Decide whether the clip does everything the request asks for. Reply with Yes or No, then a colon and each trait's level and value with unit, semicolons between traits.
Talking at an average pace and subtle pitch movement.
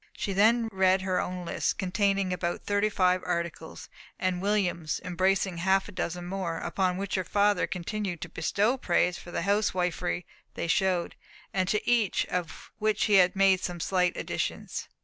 Yes: average, 170 wpm; narrow, 2.1 semitones